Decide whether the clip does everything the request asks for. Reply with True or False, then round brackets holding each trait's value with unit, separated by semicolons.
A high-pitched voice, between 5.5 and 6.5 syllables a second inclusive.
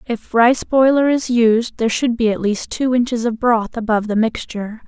False (235 Hz; 5.1 syllables/s)